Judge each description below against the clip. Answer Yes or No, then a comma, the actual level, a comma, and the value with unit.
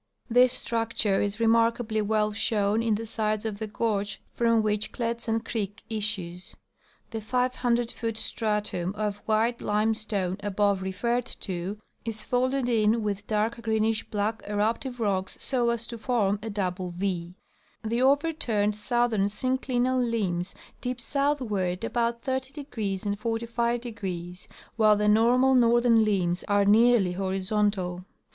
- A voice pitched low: No, high, 220 Hz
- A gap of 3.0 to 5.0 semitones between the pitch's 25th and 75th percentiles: No, narrow, 2.6 semitones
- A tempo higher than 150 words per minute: No, slow, 135 wpm